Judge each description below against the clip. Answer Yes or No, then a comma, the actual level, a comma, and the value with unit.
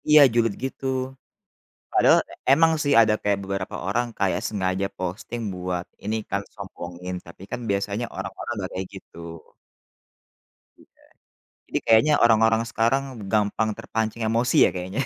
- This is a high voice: No, low, 105 Hz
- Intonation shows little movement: No, average, 3.5 semitones